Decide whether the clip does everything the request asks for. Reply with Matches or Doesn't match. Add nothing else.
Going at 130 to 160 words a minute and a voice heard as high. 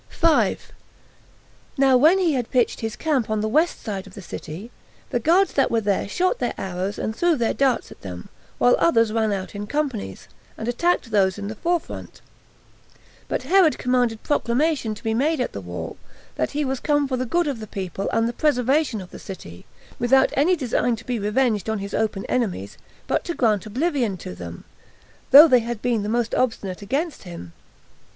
Doesn't match